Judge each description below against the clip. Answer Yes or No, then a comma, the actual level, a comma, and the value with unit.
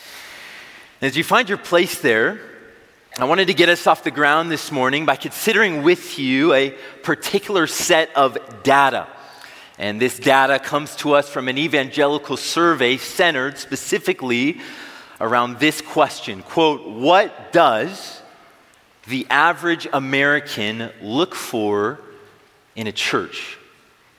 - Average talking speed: No, slow, 125 wpm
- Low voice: No, medium, 150 Hz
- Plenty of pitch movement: Yes, wide, 6.0 semitones